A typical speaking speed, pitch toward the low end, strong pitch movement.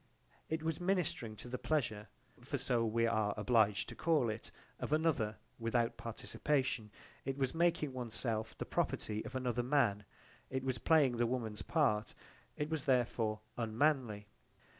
No: average, 155 wpm; low, 125 Hz; average, 4.6 semitones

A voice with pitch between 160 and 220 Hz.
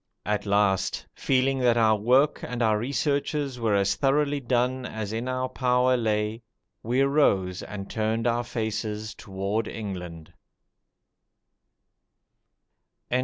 No: low, 115 Hz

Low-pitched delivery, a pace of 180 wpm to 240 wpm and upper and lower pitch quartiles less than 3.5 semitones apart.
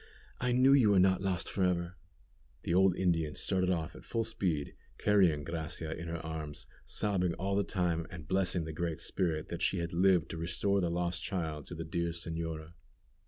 Yes: very low, 85 Hz; average, 195 wpm; narrow, 2.6 semitones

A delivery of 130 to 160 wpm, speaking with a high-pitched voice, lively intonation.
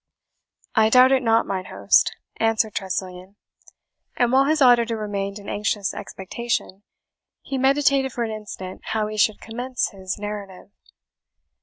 No: average, 140 wpm; high, 215 Hz; average, 3.7 semitones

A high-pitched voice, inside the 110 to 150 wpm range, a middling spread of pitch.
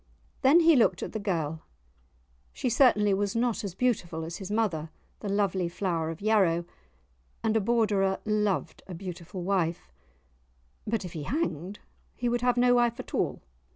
No: high, 200 Hz; average, 165 wpm; average, 5.0 semitones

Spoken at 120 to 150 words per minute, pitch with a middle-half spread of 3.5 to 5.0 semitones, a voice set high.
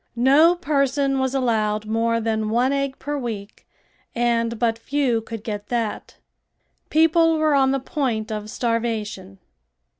Yes: average, 140 wpm; average, 3.8 semitones; high, 240 Hz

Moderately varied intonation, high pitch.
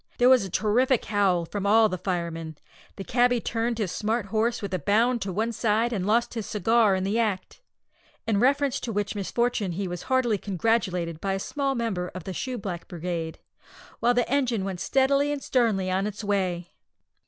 Yes: average, 4.2 semitones; high, 210 Hz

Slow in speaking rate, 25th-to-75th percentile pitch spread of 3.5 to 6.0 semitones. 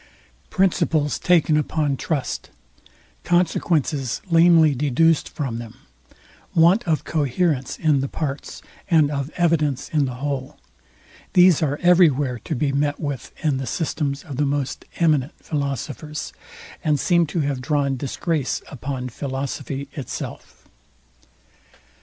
No: slow, 125 wpm; average, 3.0 semitones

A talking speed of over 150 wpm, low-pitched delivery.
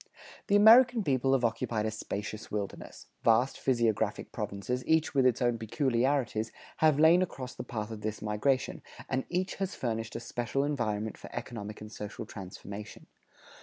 Yes: average, 160 wpm; low, 120 Hz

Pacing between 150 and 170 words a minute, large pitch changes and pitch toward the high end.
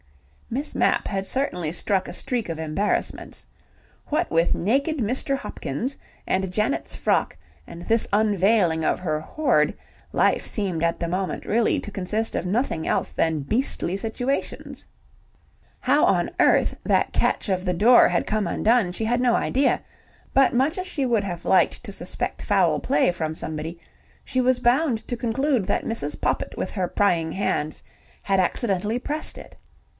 Yes: average, 160 wpm; wide, 5.8 semitones; high, 210 Hz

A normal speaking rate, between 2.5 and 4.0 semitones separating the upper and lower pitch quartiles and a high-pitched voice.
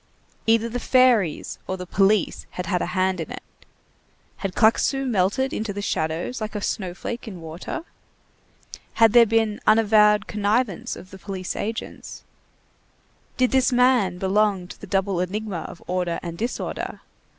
Yes: average, 155 wpm; average, 3.6 semitones; high, 205 Hz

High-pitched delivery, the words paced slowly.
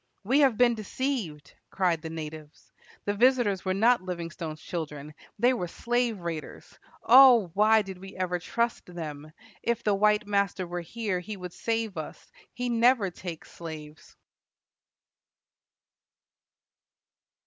Yes: high, 195 Hz; slow, 130 wpm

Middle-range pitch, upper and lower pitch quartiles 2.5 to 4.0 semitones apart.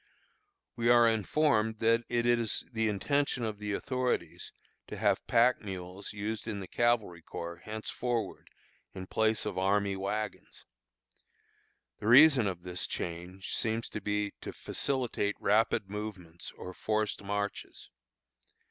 No: low, 105 Hz; average, 3.1 semitones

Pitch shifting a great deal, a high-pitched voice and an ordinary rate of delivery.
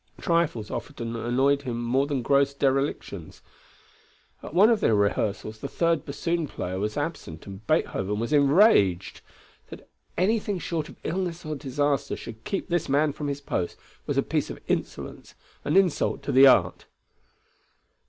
No: wide, 6.0 semitones; medium, 140 Hz; average, 155 wpm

